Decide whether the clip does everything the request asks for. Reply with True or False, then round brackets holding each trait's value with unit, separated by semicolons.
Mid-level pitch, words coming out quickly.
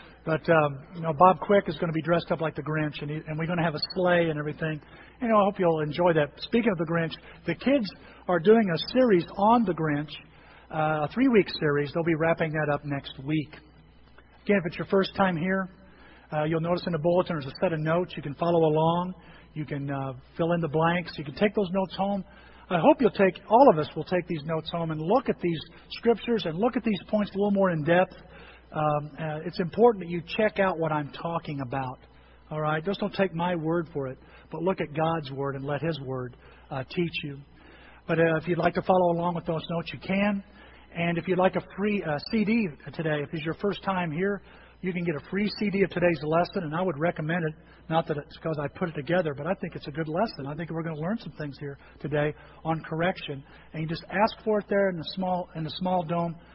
True (170 Hz; 250 wpm)